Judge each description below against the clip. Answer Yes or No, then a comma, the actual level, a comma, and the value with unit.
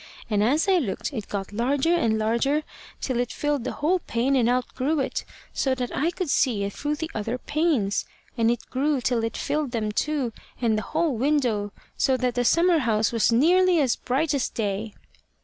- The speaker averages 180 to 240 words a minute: Yes, average, 200 wpm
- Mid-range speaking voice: No, very high, 255 Hz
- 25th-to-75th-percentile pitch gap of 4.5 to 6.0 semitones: Yes, average, 4.8 semitones